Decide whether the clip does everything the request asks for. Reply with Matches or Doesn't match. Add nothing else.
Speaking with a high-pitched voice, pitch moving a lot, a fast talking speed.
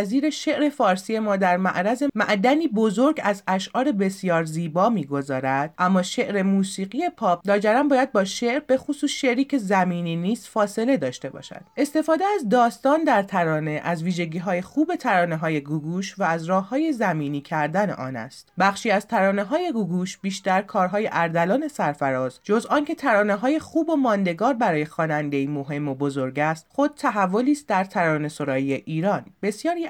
Matches